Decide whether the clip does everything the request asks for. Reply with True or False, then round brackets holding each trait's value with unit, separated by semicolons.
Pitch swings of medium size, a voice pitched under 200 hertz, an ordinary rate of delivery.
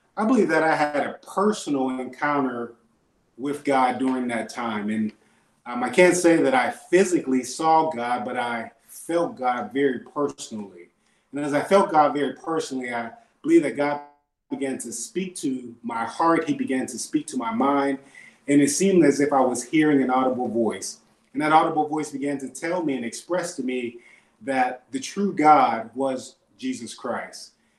True (4.3 semitones; 140 Hz; 180 wpm)